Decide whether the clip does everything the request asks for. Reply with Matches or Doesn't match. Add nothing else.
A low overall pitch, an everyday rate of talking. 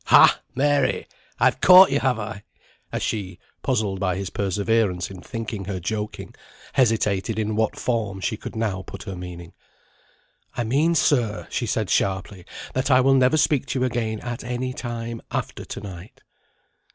Matches